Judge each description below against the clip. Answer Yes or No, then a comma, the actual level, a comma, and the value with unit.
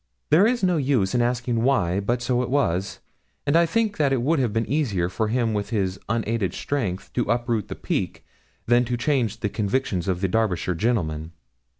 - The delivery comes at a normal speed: Yes, average, 195 wpm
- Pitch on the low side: Yes, low, 115 Hz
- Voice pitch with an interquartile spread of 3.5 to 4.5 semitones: No, average, 5.2 semitones